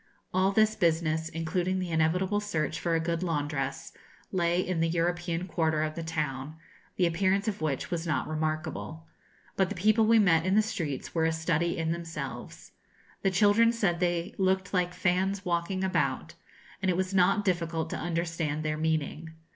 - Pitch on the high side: No, medium, 170 Hz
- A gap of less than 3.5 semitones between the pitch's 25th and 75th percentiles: Yes, narrow, 2.6 semitones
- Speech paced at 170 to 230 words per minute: Yes, average, 175 wpm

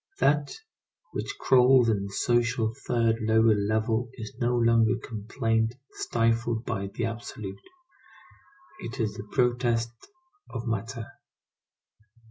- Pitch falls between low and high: No, low, 115 Hz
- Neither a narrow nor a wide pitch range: No, narrow, 1.5 semitones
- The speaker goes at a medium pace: No, slow, 110 wpm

